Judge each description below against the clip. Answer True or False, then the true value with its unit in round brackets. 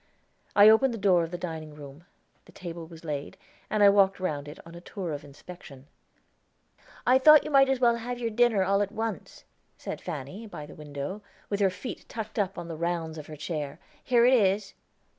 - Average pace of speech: False (210 wpm)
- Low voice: False (185 Hz)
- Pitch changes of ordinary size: False (5.7 semitones)